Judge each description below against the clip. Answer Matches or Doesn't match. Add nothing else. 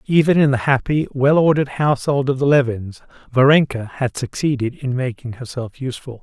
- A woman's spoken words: Doesn't match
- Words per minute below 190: Matches